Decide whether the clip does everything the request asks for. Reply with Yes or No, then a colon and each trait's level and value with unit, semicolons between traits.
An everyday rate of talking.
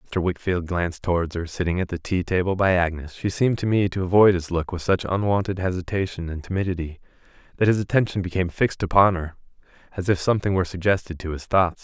No: fast, 215 wpm